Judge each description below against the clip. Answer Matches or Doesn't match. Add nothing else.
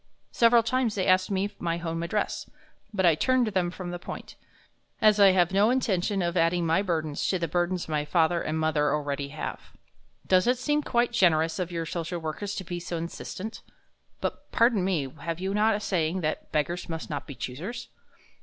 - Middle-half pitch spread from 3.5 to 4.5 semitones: Matches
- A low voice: Doesn't match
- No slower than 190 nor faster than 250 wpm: Matches